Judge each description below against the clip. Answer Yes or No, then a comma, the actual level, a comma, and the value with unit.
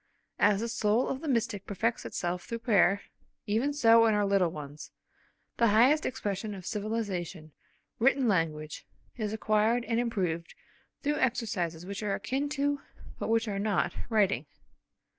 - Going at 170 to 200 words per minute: No, average, 150 wpm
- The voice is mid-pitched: No, high, 215 Hz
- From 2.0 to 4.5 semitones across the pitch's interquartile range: Yes, average, 3.5 semitones